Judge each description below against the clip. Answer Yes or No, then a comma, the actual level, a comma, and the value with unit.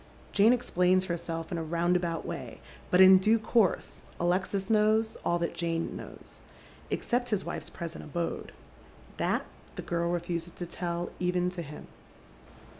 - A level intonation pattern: Yes, narrow, 2.1 semitones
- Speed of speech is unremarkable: Yes, average, 145 wpm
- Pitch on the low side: No, medium, 180 Hz